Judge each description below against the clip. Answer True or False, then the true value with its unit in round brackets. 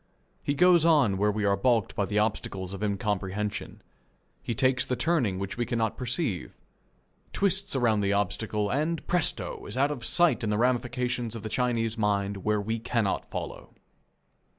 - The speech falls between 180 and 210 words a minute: False (170 wpm)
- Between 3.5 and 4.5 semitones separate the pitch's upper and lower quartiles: True (3.9 semitones)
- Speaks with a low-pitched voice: True (115 Hz)